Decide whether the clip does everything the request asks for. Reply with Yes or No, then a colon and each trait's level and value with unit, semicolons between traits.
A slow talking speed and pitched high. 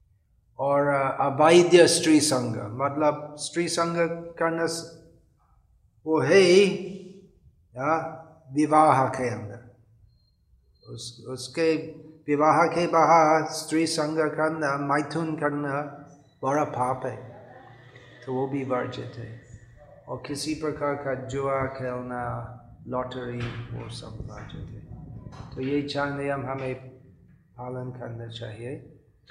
No: slow, 100 wpm; medium, 140 Hz